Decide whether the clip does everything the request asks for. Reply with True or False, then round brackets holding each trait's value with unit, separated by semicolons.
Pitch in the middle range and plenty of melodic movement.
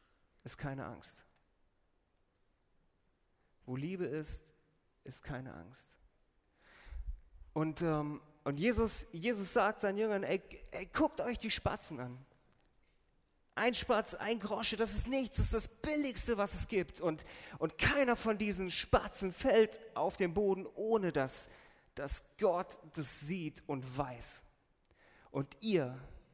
True (175 Hz; 8.2 semitones)